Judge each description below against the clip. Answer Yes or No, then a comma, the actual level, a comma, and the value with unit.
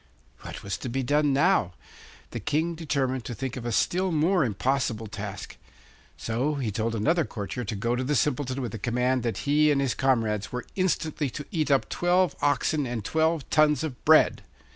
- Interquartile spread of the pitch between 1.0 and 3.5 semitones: No, average, 4.5 semitones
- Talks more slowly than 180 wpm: No, average, 190 wpm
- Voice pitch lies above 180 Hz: No, low, 135 Hz